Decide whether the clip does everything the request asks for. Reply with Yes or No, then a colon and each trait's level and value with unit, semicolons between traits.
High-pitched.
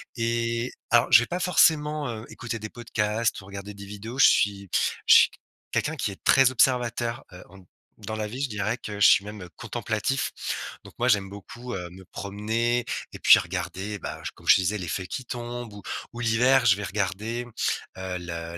No: low, 110 Hz